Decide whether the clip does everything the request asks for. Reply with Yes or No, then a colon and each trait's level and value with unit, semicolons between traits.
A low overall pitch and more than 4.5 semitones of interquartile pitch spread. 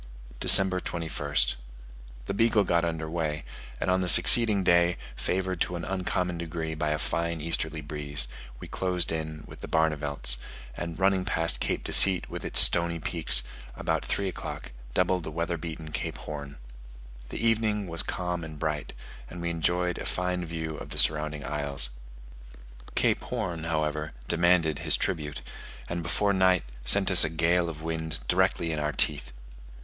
No: very low, 85 Hz; average, 2.7 semitones